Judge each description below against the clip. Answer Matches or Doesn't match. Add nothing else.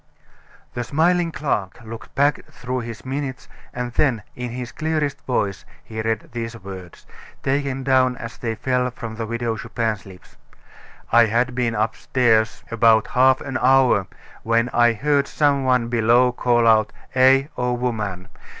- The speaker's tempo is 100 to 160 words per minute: Matches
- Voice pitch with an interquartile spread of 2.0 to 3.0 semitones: Matches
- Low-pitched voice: Matches